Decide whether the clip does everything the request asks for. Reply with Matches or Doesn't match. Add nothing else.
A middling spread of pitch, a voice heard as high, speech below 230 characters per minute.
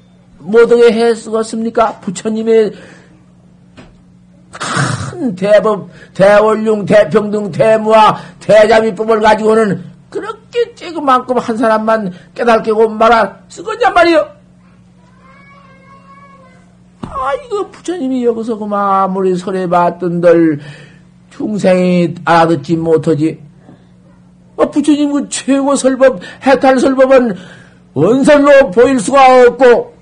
Doesn't match